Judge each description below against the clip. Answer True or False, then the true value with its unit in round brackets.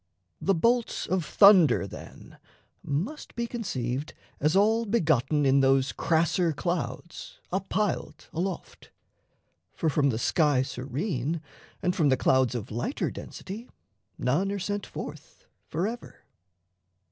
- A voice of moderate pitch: True (165 Hz)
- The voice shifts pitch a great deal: True (6.7 semitones)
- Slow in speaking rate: True (125 wpm)